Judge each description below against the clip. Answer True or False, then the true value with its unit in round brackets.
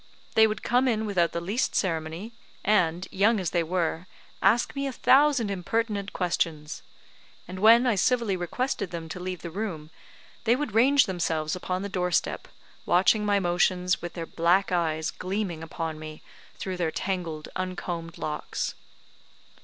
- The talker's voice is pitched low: False (185 Hz)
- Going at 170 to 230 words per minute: False (160 wpm)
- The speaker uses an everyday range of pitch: True (4.1 semitones)